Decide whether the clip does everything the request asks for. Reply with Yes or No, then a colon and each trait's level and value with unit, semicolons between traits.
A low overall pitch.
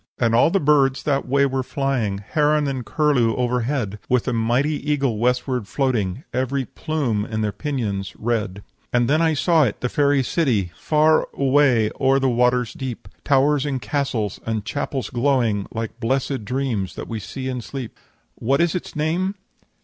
Yes: low, 130 Hz